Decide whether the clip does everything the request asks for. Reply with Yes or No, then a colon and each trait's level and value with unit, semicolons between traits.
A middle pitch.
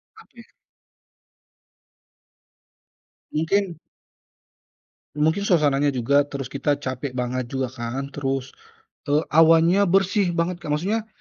Yes: medium, 145 Hz